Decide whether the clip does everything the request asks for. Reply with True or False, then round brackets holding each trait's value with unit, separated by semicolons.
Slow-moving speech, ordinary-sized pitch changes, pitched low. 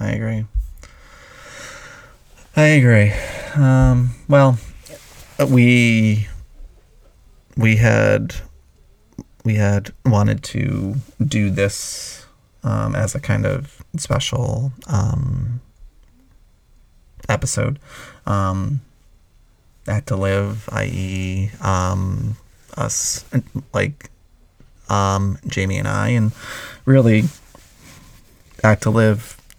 True (80 wpm; 4.6 semitones; 110 Hz)